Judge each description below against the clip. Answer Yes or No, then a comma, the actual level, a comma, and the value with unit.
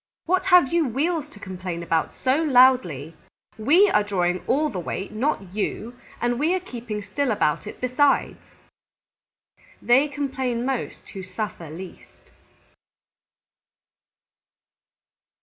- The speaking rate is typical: No, slow, 120 wpm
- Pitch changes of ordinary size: No, wide, 7.1 semitones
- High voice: Yes, high, 240 Hz